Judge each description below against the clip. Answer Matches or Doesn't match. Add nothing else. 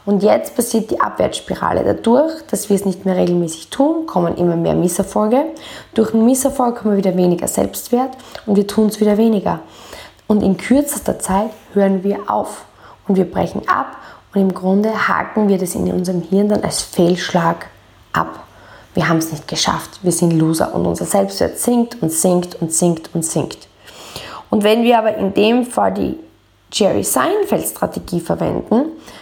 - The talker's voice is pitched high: Matches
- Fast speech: Doesn't match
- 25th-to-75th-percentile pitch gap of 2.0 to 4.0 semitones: Doesn't match